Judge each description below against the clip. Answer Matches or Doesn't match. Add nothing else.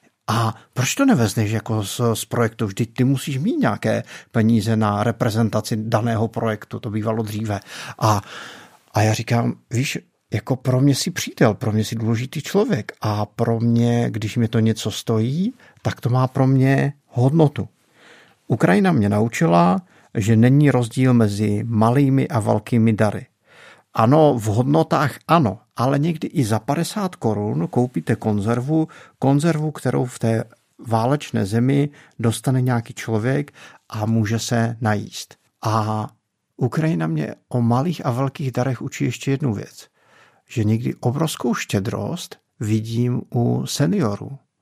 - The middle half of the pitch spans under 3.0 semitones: Doesn't match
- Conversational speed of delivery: Matches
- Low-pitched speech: Matches